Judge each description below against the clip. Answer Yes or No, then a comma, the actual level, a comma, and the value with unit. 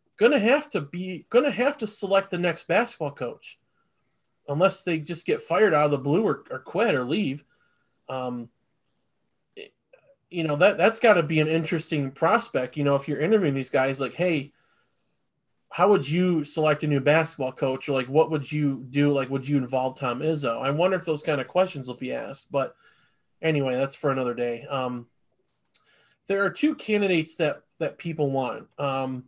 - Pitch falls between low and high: Yes, medium, 150 Hz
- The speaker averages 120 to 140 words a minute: No, average, 190 wpm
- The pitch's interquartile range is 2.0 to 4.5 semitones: No, average, 4.9 semitones